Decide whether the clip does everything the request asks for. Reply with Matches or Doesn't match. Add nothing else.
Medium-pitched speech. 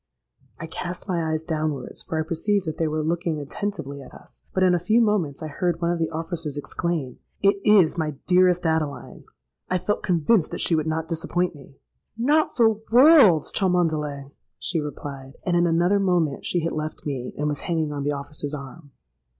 Matches